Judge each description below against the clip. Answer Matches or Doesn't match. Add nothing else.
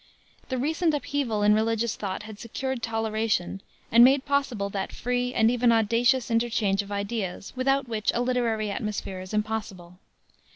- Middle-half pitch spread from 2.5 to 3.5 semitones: Matches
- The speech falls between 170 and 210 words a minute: Doesn't match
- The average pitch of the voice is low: Doesn't match